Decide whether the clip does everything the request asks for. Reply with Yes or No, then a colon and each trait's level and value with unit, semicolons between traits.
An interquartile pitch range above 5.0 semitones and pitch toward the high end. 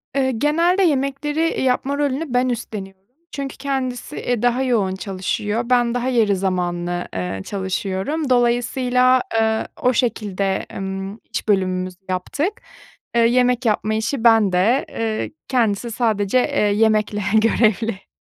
No: average, 4.6 semitones; high, 230 Hz